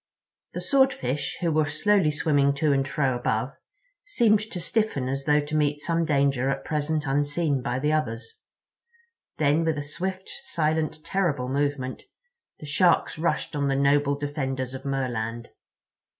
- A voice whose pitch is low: No, medium, 145 Hz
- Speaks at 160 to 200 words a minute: No, average, 150 wpm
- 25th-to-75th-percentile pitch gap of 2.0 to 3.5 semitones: Yes, average, 2.7 semitones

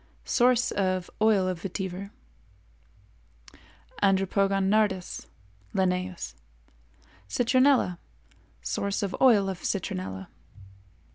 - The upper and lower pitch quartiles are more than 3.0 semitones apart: No, narrow, 2.6 semitones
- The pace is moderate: No, slow, 75 wpm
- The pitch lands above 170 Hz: Yes, high, 190 Hz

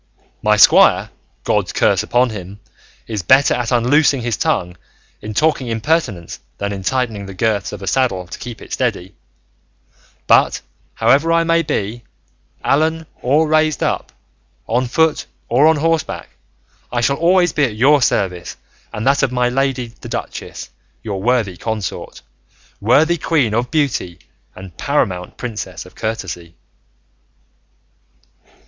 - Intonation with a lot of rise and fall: Yes, wide, 5.9 semitones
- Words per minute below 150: Yes, average, 140 wpm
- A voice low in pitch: Yes, low, 120 Hz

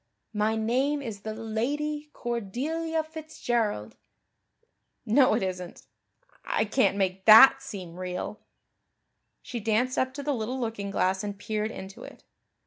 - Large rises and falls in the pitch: No, average, 4.9 semitones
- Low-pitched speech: No, high, 225 Hz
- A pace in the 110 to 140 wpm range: Yes, slow, 135 wpm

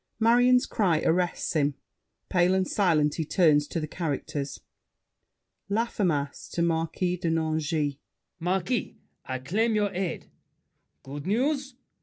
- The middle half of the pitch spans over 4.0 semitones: Yes, average, 4.8 semitones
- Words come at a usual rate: No, slow, 120 wpm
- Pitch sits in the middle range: Yes, medium, 170 Hz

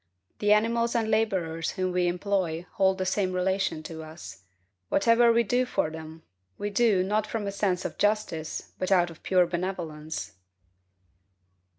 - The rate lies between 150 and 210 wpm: Yes, average, 160 wpm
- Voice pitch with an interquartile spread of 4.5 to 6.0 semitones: No, average, 4.0 semitones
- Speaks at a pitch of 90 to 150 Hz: No, high, 190 Hz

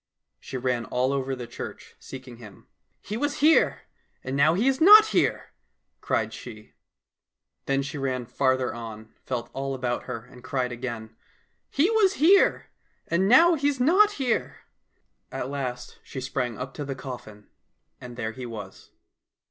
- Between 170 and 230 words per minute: Yes, average, 175 wpm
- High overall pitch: No, low, 130 Hz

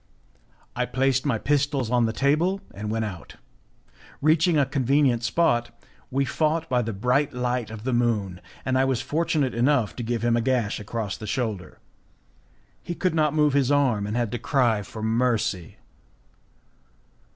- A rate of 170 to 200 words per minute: Yes, average, 175 wpm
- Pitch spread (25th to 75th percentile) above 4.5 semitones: No, average, 4.0 semitones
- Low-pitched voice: Yes, low, 125 Hz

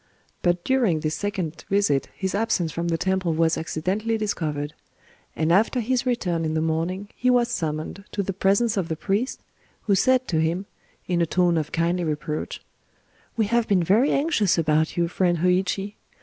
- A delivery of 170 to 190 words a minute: Yes, average, 180 wpm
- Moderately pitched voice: Yes, medium, 180 Hz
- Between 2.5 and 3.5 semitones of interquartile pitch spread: No, average, 4.2 semitones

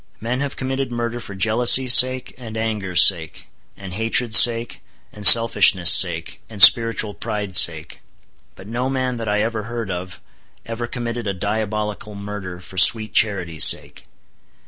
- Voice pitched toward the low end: Yes, low, 110 Hz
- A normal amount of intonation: Yes, average, 3.5 semitones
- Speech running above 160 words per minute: No, average, 150 wpm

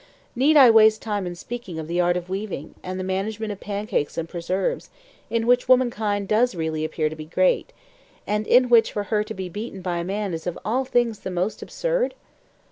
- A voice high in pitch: Yes, high, 205 Hz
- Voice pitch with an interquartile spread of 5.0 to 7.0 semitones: No, average, 4.4 semitones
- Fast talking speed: Yes, fast, 210 wpm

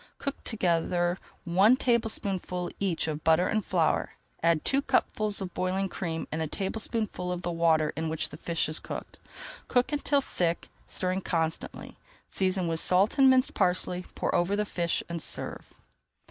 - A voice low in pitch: No, medium, 180 Hz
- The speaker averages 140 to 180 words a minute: Yes, average, 165 wpm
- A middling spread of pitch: Yes, average, 3.6 semitones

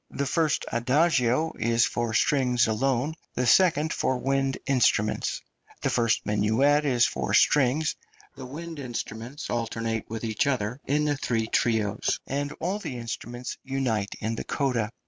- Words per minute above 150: No, average, 145 wpm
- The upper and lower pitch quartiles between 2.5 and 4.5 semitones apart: Yes, average, 3.7 semitones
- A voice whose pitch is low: Yes, low, 125 Hz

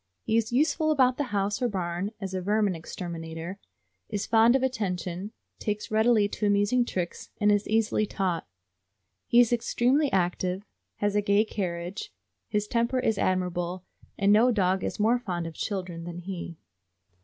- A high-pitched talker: Yes, high, 205 Hz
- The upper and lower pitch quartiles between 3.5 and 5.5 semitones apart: Yes, average, 3.9 semitones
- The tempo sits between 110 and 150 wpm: No, average, 165 wpm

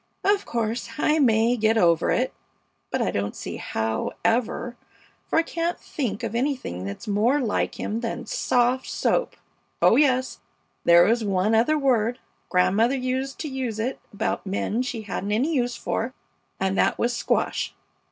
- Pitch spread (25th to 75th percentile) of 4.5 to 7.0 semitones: No, average, 3.7 semitones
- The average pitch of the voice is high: Yes, high, 235 Hz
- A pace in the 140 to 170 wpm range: Yes, average, 160 wpm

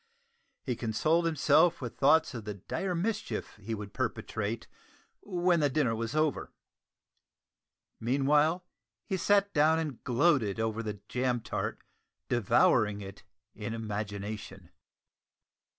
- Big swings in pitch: Yes, wide, 6.7 semitones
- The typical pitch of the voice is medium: No, low, 125 Hz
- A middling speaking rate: No, slow, 120 wpm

